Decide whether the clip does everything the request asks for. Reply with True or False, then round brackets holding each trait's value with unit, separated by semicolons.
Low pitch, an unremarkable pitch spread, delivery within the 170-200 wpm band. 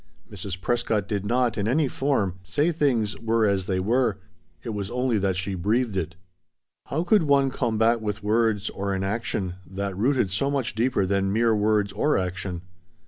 True (105 Hz; 4.0 semitones; 180 wpm)